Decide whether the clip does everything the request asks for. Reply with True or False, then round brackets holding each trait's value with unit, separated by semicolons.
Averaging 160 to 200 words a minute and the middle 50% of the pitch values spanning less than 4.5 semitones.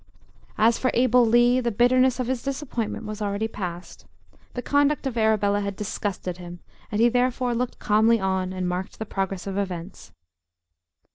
True (165 wpm; 4.1 semitones)